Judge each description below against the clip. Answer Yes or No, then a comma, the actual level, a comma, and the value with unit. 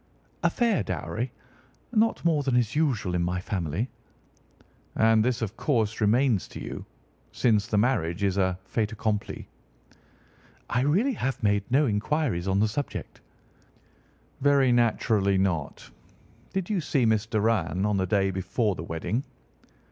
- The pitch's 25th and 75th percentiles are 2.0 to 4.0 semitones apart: No, average, 5.1 semitones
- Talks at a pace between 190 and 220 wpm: No, average, 145 wpm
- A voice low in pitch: Yes, low, 110 Hz